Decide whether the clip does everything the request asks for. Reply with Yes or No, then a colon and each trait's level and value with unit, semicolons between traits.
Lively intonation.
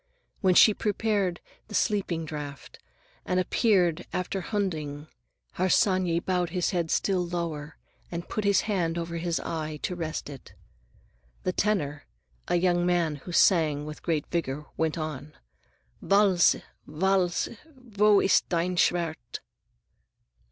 No: average, 3.2 semitones